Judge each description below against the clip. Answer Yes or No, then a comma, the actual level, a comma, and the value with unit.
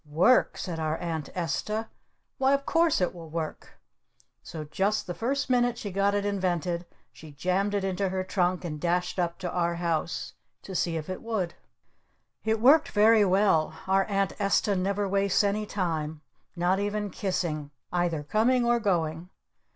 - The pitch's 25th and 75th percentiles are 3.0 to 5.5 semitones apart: Yes, average, 3.4 semitones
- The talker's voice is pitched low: No, medium, 185 Hz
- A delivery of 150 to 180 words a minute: Yes, average, 165 wpm